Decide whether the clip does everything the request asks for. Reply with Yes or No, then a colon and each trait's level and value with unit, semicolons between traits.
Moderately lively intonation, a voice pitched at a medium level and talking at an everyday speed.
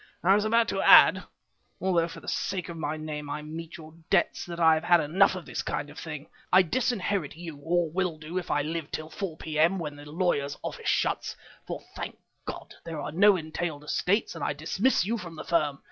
No: average, 3.0 semitones; medium, 165 Hz; fast, 220 wpm